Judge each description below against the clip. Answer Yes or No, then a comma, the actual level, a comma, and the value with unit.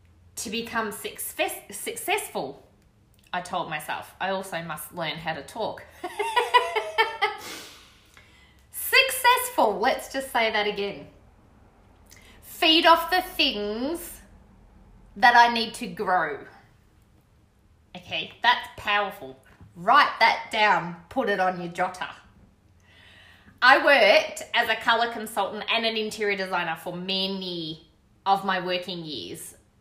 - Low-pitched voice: No, high, 205 Hz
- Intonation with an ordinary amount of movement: No, wide, 9.0 semitones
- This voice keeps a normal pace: No, slow, 115 wpm